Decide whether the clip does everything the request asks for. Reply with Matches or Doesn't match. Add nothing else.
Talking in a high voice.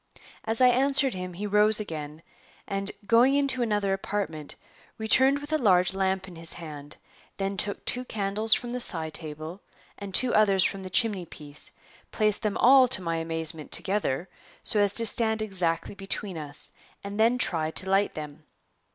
Matches